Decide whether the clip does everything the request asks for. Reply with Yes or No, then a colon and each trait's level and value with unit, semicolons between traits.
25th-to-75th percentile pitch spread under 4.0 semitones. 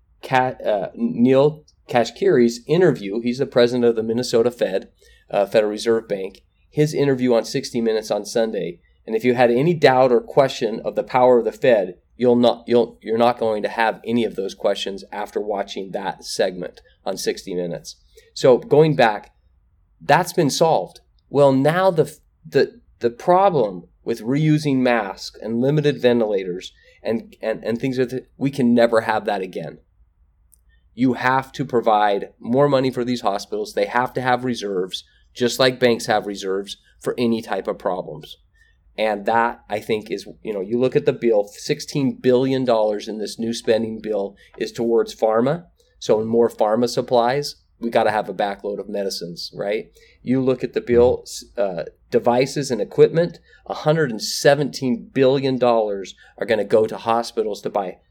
Yes: average, 3.4 semitones